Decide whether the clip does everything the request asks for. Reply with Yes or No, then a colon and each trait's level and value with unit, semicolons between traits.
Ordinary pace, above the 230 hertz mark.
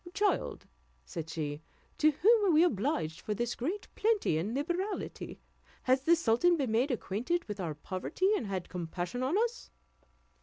Yes: average, 160 wpm; very high, 255 Hz